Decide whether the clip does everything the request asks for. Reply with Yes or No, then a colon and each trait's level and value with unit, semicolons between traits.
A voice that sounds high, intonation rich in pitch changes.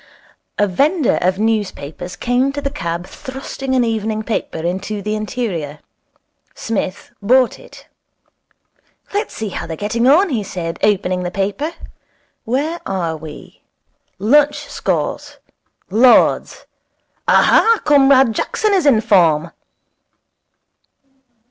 Yes: high, 220 Hz; wide, 6.5 semitones